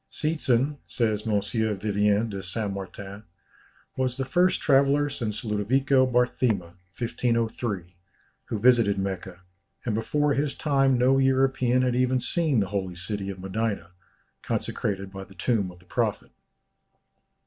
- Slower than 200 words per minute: Yes, slow, 135 wpm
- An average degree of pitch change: Yes, average, 4.9 semitones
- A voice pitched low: Yes, low, 115 Hz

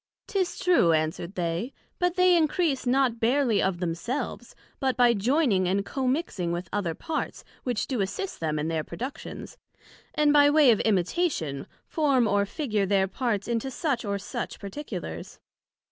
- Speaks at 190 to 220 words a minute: No, average, 160 wpm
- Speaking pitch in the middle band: No, high, 235 Hz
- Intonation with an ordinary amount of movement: No, wide, 7.1 semitones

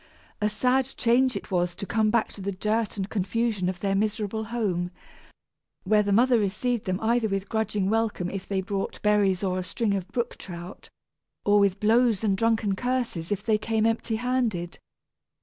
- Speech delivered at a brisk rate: No, average, 185 wpm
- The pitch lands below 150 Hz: No, high, 210 Hz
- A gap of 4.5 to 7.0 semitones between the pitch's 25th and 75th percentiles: No, average, 2.9 semitones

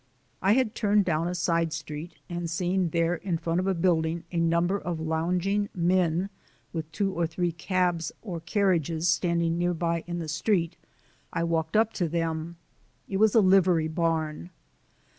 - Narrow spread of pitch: Yes, narrow, 2.0 semitones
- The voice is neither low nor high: Yes, medium, 170 Hz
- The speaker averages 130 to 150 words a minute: No, average, 165 wpm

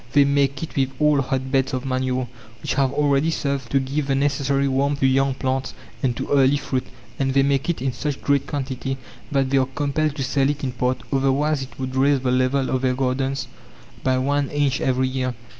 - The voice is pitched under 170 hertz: Yes, low, 135 Hz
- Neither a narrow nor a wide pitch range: No, narrow, 1.2 semitones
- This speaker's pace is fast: Yes, fast, 215 wpm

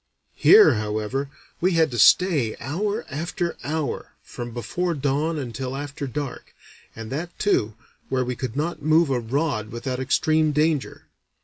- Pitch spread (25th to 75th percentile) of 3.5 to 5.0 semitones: Yes, average, 4.5 semitones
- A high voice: No, medium, 140 Hz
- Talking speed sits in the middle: Yes, average, 145 wpm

